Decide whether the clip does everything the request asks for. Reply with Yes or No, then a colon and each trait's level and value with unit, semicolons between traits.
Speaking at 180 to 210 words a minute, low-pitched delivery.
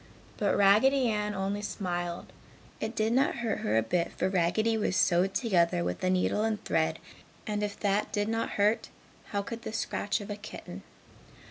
No: average, 185 wpm; high, 205 Hz